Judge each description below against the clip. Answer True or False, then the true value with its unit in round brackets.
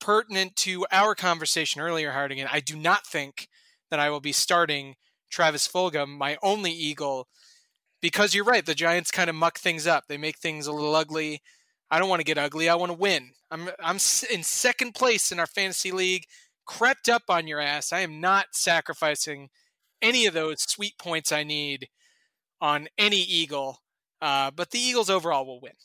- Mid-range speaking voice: True (170 Hz)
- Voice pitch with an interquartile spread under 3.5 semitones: False (4.5 semitones)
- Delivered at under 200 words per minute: True (190 wpm)